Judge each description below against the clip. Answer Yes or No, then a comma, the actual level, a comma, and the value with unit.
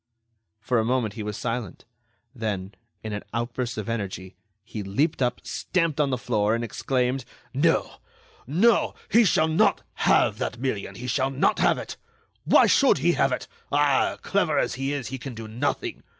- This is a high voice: No, low, 125 Hz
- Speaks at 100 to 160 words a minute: No, average, 180 wpm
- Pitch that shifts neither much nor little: Yes, average, 4.0 semitones